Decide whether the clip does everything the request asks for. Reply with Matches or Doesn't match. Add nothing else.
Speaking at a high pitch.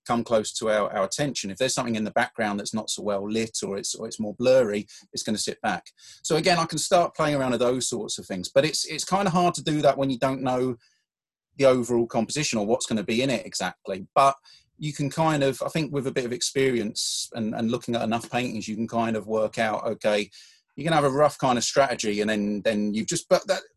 Doesn't match